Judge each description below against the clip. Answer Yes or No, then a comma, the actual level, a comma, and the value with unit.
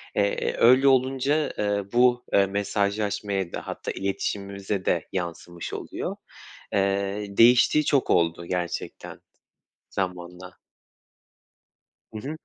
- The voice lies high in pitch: No, low, 100 Hz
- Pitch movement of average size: Yes, average, 4.6 semitones